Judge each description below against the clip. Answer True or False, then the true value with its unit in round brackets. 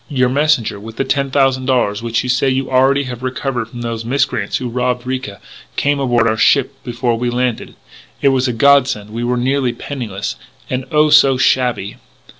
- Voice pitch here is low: True (125 Hz)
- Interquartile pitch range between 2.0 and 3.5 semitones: True (2.4 semitones)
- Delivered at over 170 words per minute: True (190 wpm)